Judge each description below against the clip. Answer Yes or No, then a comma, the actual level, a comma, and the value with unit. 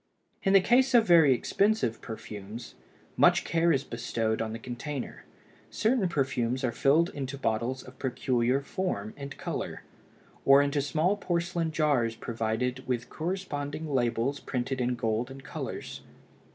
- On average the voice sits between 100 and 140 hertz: Yes, low, 135 Hz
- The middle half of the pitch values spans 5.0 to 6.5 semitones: Yes, wide, 5.4 semitones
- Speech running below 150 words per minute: Yes, average, 140 wpm